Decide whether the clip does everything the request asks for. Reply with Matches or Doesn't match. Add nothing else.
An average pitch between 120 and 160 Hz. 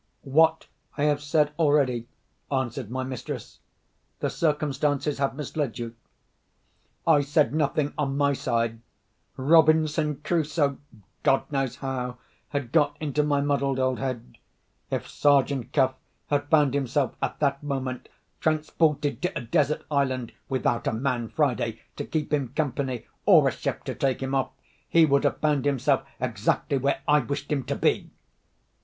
Matches